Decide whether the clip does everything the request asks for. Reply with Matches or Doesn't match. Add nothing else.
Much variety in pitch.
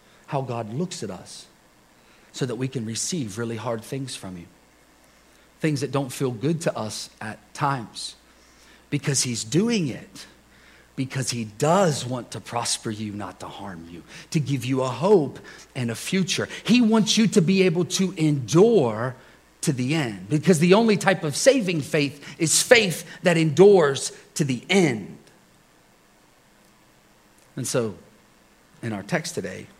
Matches